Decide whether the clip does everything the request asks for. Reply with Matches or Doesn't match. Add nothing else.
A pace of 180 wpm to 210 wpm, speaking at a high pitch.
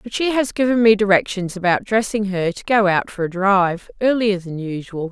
Matches